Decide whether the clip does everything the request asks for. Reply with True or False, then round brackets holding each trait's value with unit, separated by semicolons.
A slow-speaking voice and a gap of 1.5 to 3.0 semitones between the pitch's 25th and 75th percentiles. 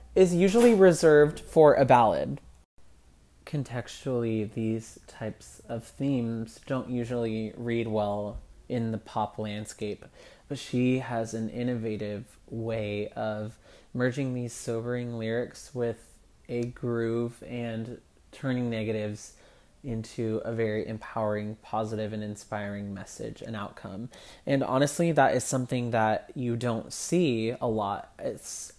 True (120 wpm; 2.4 semitones)